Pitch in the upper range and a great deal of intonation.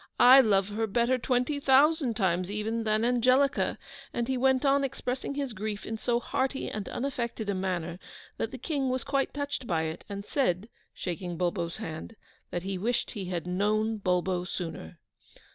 Yes: high, 220 Hz; wide, 5.7 semitones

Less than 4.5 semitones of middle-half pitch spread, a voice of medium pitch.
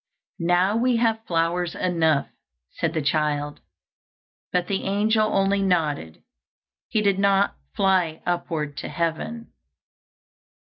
Yes: average, 3.8 semitones; medium, 180 Hz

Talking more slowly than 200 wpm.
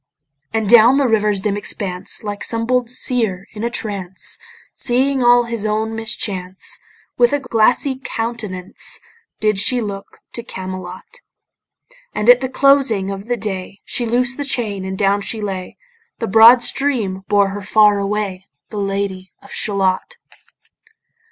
Yes: average, 150 wpm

